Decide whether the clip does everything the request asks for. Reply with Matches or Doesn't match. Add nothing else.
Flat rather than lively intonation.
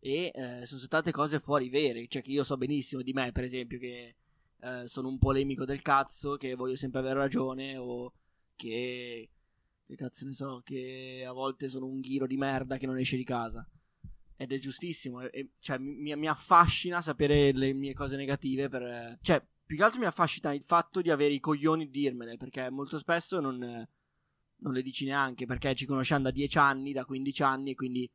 Matches